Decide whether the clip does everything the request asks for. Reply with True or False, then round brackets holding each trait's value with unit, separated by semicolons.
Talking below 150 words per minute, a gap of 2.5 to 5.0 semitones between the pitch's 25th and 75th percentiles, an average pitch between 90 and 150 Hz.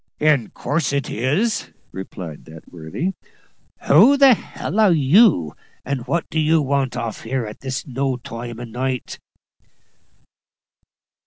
False (140 wpm; 5.4 semitones; 135 Hz)